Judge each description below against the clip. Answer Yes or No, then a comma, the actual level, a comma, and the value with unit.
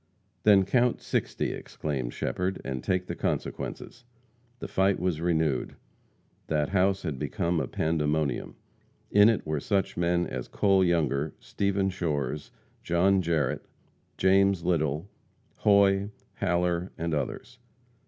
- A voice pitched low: Yes, very low, 90 Hz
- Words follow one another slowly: Yes, slow, 125 wpm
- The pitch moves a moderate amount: Yes, average, 3.9 semitones